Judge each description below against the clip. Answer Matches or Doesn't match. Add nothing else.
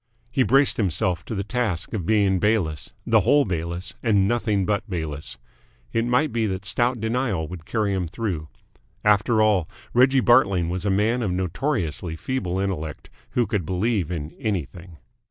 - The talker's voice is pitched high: Doesn't match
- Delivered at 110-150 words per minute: Doesn't match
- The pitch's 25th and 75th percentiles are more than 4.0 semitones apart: Matches